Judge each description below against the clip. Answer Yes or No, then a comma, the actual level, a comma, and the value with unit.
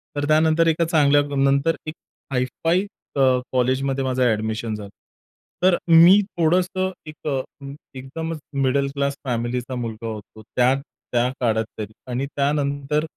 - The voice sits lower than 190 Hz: Yes, medium, 140 Hz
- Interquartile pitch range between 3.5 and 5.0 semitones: Yes, average, 4.0 semitones